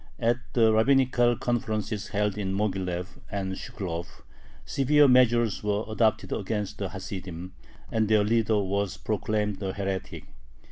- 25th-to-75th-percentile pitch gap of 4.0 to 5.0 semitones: No, average, 2.7 semitones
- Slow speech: Yes, slow, 130 wpm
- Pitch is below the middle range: Yes, low, 105 Hz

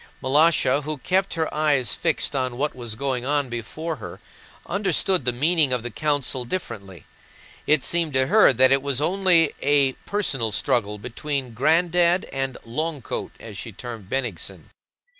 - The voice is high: No, medium, 140 Hz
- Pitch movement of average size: Yes, average, 4.6 semitones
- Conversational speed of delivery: Yes, average, 160 wpm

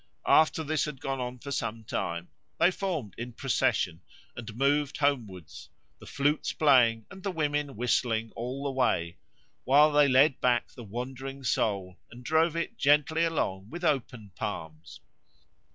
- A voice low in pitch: Yes, low, 130 Hz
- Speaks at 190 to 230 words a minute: No, average, 150 wpm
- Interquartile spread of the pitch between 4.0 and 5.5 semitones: Yes, average, 4.5 semitones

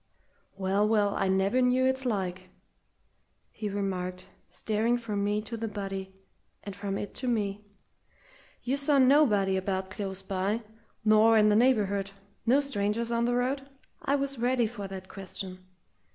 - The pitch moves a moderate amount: Yes, average, 3.8 semitones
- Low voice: No, high, 210 Hz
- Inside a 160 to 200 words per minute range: No, average, 150 wpm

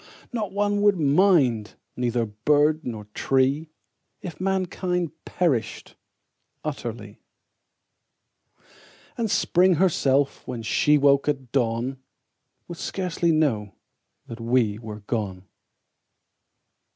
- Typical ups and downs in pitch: No, wide, 7.1 semitones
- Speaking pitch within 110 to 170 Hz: Yes, medium, 140 Hz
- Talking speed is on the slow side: Yes, slow, 95 wpm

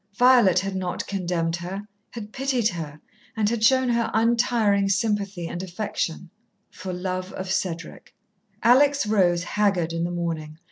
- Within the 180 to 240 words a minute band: No, average, 145 wpm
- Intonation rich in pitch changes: No, average, 4.2 semitones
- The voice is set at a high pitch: Yes, high, 195 Hz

